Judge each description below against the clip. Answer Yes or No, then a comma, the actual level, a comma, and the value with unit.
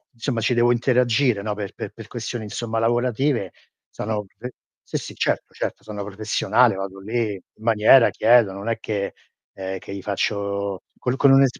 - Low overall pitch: Yes, low, 110 Hz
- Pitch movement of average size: Yes, average, 3.2 semitones